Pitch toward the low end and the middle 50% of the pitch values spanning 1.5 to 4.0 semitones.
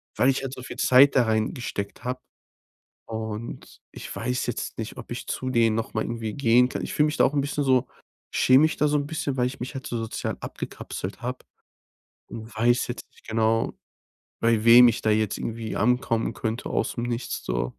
Yes: low, 120 Hz; narrow, 2.6 semitones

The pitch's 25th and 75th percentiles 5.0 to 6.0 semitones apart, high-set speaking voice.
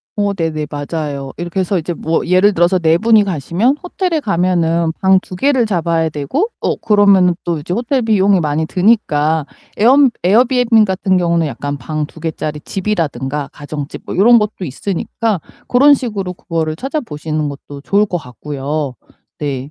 No: wide, 5.5 semitones; medium, 175 Hz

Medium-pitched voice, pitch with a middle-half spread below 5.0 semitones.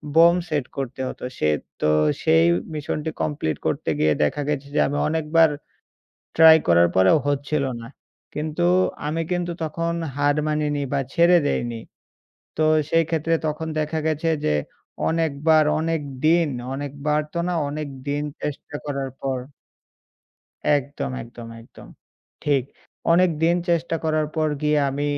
Yes: medium, 150 Hz; narrow, 2.5 semitones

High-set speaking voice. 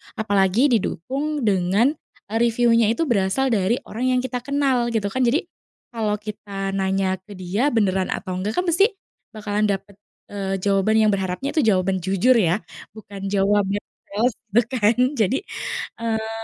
Yes: high, 210 Hz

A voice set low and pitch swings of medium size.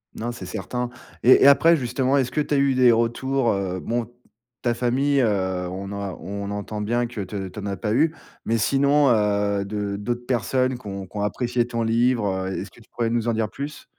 Yes: low, 115 Hz; average, 3.9 semitones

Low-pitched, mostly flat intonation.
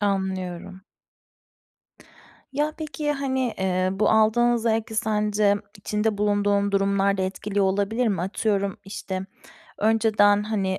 No: high, 205 Hz; narrow, 2.2 semitones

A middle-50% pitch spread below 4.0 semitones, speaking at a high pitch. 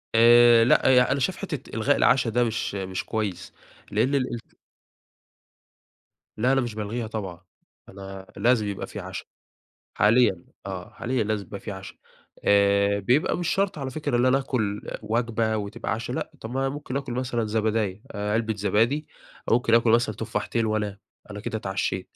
No: average, 3.3 semitones; low, 110 Hz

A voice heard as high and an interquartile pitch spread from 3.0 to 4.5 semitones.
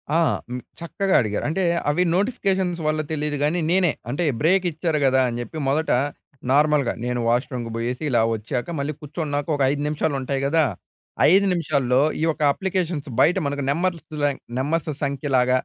No: medium, 150 Hz; average, 4.0 semitones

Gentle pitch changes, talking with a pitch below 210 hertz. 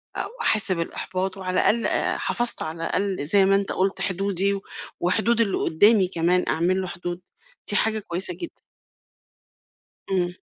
Yes: narrow, 2.2 semitones; high, 190 Hz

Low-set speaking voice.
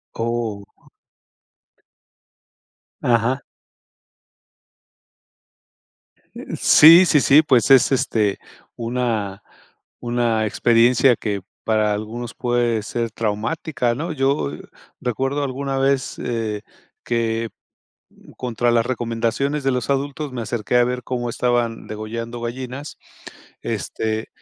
Yes: low, 120 Hz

